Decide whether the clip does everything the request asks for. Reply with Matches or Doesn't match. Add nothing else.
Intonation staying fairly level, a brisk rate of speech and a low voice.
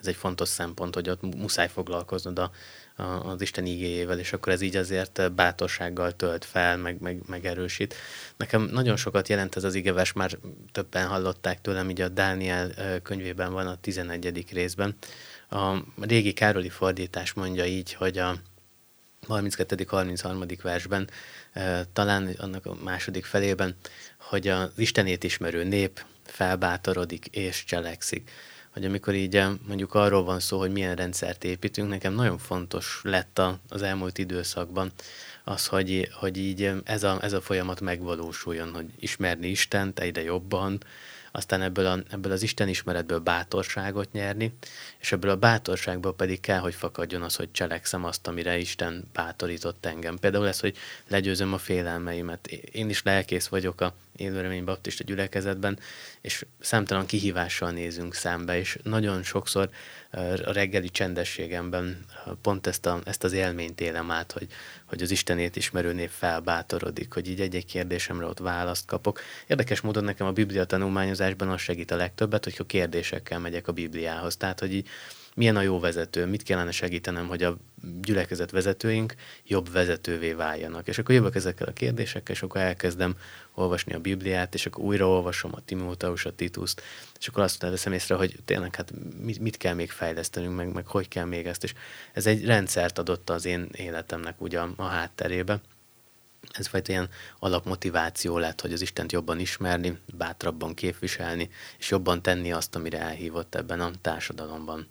Matches